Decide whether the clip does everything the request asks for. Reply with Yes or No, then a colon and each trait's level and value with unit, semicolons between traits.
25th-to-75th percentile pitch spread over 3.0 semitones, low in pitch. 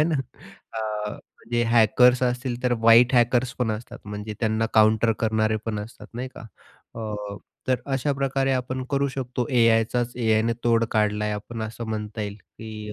No: narrow, 2.4 semitones; low, 115 Hz